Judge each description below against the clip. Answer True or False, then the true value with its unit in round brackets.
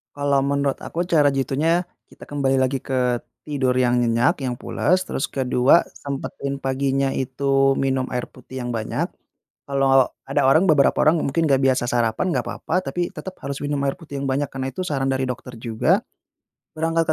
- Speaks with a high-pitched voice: False (135 Hz)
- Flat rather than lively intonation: True (1.9 semitones)